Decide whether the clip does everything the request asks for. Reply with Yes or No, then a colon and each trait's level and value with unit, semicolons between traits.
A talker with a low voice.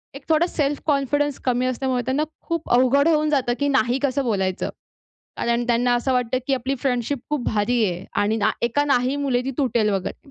No: very high, 255 Hz